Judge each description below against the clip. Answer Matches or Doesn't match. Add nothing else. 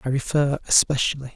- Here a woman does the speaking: Doesn't match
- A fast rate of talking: Doesn't match